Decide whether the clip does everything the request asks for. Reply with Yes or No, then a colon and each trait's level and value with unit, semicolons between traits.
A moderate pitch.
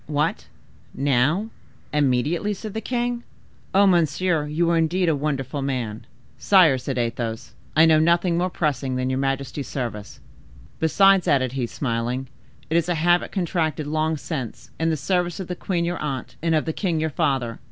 Yes: medium, 155 Hz